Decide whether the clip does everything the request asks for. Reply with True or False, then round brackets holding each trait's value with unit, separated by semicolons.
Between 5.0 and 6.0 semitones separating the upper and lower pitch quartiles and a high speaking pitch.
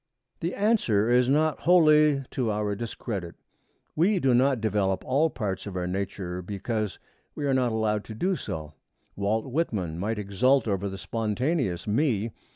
False (5.6 semitones; 110 Hz)